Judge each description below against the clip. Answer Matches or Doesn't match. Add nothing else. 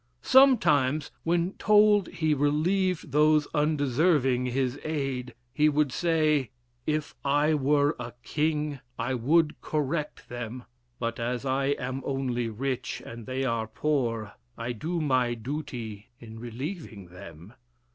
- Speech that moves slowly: Matches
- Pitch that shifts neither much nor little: Matches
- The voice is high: Doesn't match